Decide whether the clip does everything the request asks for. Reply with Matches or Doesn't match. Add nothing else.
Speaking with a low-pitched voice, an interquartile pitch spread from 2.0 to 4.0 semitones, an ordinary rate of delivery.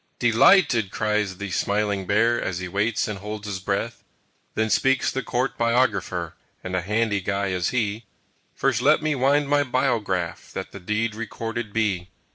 Matches